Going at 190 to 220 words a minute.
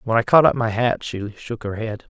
No: fast, 280 wpm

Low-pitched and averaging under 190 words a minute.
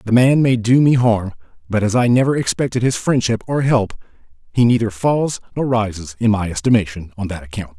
No: low, 110 Hz; average, 200 wpm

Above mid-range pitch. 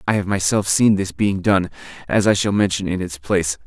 No: very low, 95 Hz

